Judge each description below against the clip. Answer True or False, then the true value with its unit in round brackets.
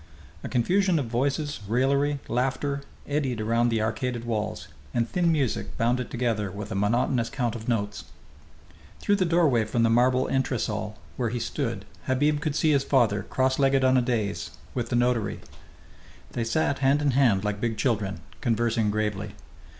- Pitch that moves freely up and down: False (3.6 semitones)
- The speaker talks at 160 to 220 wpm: True (170 wpm)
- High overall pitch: False (120 Hz)